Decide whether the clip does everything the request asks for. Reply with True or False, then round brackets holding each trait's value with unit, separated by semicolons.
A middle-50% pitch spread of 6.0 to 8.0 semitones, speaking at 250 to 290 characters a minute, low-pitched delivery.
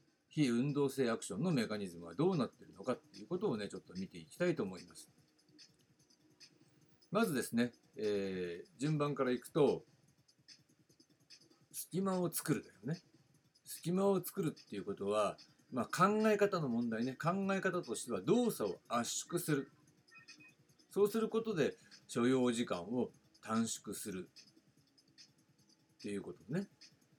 False (6.9 semitones; 280 characters per minute; 150 Hz)